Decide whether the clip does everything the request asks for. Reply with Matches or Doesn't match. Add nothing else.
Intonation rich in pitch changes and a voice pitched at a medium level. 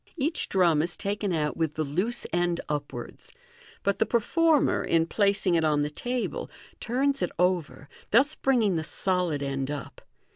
Matches